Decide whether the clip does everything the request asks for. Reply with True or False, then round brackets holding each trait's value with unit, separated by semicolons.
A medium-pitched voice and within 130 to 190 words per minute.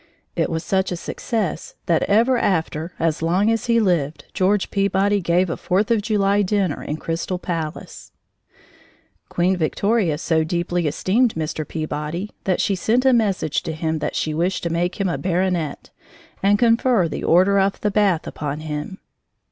True (180 Hz; 170 wpm)